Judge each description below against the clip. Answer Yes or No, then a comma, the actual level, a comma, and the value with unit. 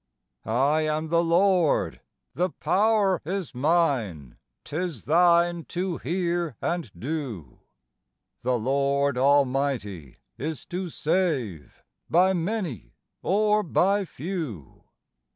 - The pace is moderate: No, slow, 100 wpm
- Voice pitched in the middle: Yes, medium, 160 Hz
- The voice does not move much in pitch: No, wide, 5.4 semitones